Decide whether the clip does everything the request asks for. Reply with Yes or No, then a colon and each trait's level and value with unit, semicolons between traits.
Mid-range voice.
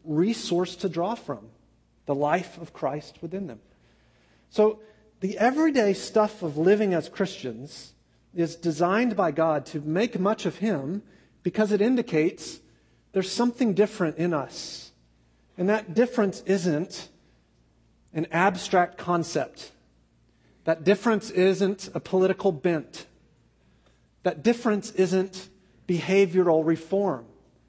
Yes: medium, 180 Hz